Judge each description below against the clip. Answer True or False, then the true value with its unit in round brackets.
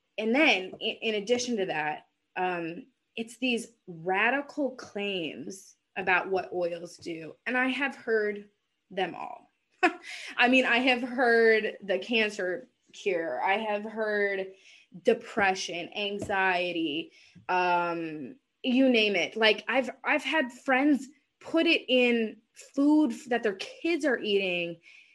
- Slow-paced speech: True (125 wpm)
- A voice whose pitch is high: True (225 Hz)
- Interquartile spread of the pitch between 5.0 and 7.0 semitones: True (5.5 semitones)